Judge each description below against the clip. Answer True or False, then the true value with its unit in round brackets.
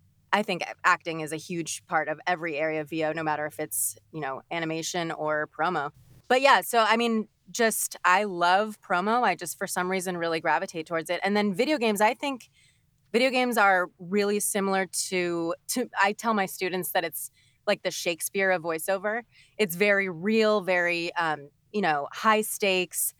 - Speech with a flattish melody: False (4.6 semitones)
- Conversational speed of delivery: True (185 wpm)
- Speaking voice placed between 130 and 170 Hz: False (180 Hz)